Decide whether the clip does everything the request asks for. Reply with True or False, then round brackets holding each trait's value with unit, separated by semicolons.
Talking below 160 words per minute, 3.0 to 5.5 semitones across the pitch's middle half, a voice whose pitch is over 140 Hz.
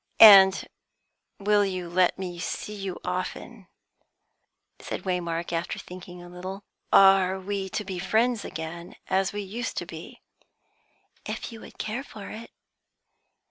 False (140 wpm; 2.4 semitones; 190 Hz)